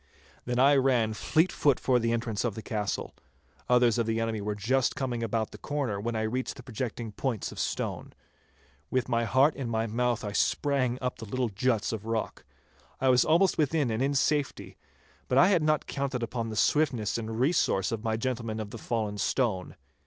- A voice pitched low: Yes, low, 120 Hz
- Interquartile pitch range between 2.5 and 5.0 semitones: Yes, average, 3.0 semitones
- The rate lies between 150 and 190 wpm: No, average, 200 wpm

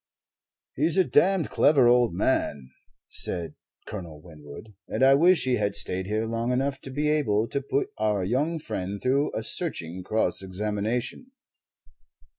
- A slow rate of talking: No, average, 150 wpm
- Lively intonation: Yes, wide, 6.7 semitones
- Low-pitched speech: Yes, low, 115 Hz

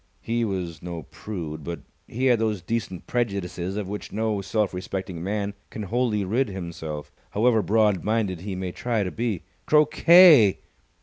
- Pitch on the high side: No, low, 100 Hz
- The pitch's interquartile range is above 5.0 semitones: No, average, 3.7 semitones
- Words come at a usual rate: Yes, average, 160 wpm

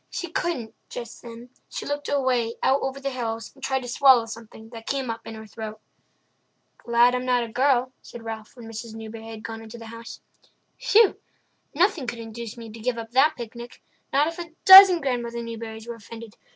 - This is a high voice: Yes, high, 235 Hz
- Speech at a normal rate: Yes, average, 195 wpm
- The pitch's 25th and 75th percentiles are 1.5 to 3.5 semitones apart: Yes, average, 2.9 semitones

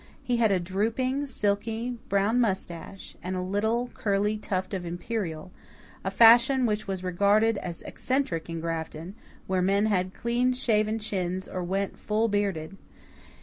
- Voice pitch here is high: Yes, high, 200 Hz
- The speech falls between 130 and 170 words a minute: Yes, average, 150 wpm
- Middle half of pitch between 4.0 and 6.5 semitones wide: No, average, 3.6 semitones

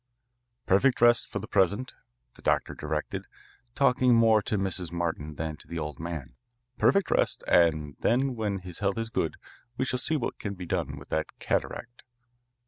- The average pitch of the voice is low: Yes, low, 100 Hz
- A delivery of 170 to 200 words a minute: Yes, average, 175 wpm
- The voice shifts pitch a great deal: Yes, wide, 6.1 semitones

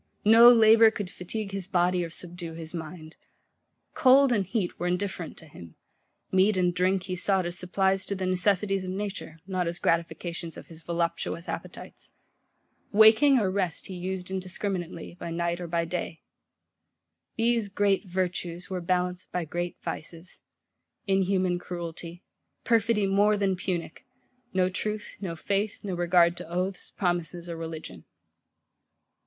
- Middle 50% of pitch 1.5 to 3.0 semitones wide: Yes, narrow, 2.5 semitones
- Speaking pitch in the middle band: Yes, medium, 180 Hz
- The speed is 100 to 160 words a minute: Yes, average, 150 wpm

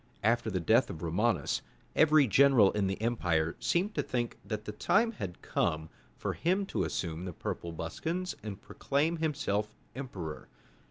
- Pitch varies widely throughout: Yes, wide, 8.0 semitones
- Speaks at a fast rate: No, average, 160 wpm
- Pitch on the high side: No, low, 110 Hz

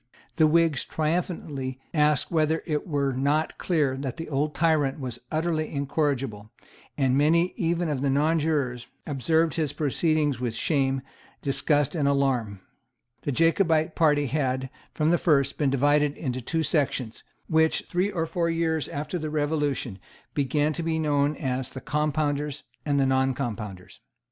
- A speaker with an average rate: Yes, average, 150 wpm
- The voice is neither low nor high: Yes, medium, 150 Hz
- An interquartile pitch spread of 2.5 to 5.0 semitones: Yes, average, 2.9 semitones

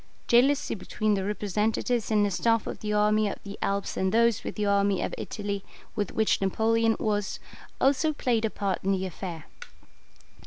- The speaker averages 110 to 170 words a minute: No, average, 180 wpm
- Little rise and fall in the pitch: Yes, narrow, 2.2 semitones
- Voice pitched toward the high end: Yes, high, 210 Hz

